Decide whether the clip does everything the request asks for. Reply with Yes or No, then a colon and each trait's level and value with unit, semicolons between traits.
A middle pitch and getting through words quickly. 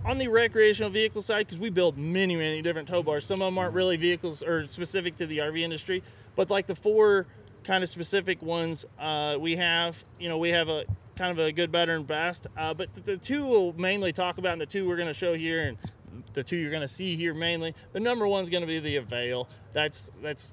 Yes: medium, 170 Hz; fast, 245 wpm